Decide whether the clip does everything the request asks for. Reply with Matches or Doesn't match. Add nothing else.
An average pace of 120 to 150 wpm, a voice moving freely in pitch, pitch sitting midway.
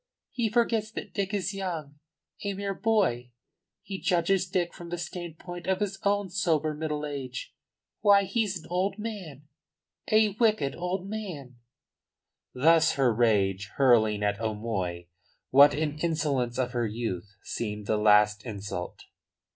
Matches